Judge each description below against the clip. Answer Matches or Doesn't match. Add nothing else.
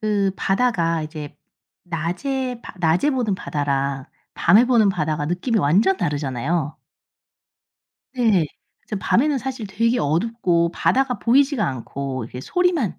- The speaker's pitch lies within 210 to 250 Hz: Doesn't match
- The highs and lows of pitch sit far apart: Matches